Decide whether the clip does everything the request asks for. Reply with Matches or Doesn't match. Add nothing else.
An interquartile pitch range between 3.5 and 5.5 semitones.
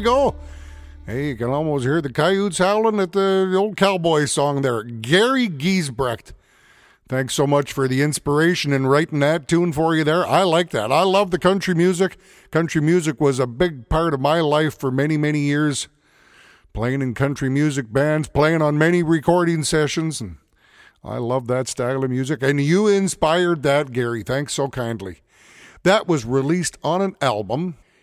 Matches